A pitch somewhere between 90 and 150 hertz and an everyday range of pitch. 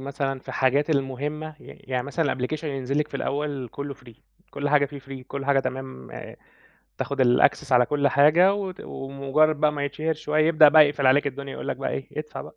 No: medium, 140 Hz; narrow, 2.0 semitones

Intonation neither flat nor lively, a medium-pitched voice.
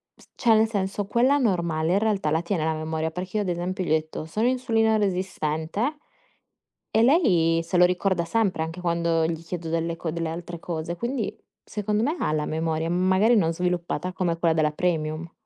Yes: average, 4.1 semitones; medium, 175 Hz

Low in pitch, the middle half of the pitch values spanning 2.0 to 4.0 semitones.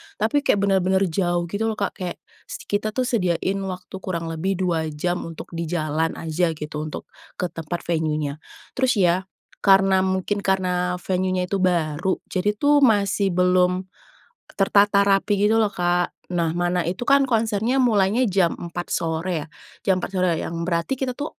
No: medium, 185 Hz; average, 2.9 semitones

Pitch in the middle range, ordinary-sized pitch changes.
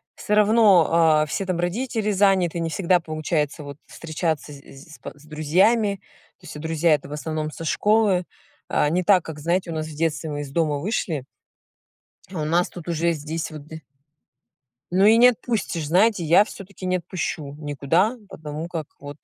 Yes: medium, 165 Hz; average, 3.7 semitones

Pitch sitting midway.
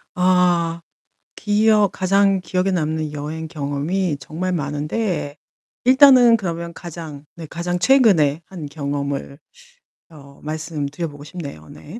Yes: medium, 165 Hz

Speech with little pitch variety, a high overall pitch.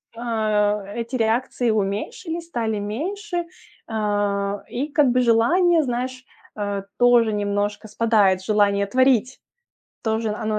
No: average, 3.5 semitones; high, 225 Hz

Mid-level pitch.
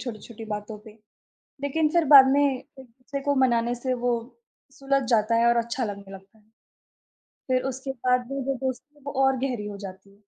No: very high, 250 Hz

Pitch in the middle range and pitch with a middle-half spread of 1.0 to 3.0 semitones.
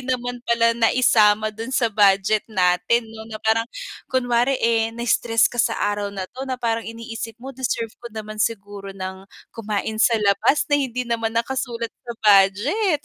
No: high, 230 Hz; narrow, 2.4 semitones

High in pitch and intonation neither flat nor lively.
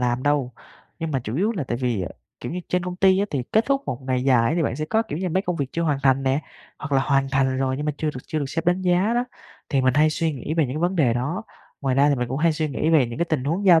No: medium, 150 Hz; average, 4.7 semitones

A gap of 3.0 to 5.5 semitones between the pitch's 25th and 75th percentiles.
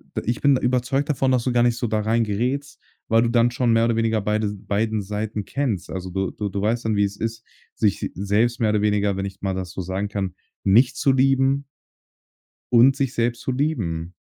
Yes: average, 3.4 semitones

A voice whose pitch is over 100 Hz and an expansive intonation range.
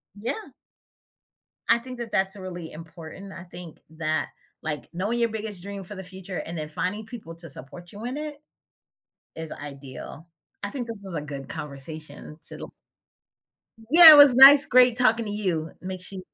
Yes: high, 190 Hz; wide, 6.1 semitones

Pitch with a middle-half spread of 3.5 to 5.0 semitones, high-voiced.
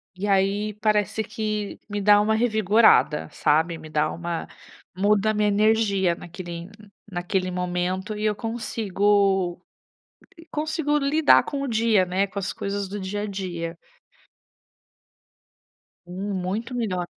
No: average, 2.9 semitones; high, 200 Hz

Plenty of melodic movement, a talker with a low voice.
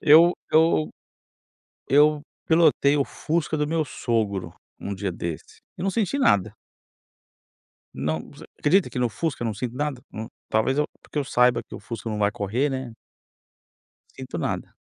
Yes: wide, 6.1 semitones; low, 130 Hz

